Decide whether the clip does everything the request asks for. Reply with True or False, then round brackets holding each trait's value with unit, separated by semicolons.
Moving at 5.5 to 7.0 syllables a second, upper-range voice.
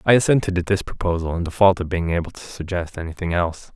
False (6.6 syllables/s; 90 Hz)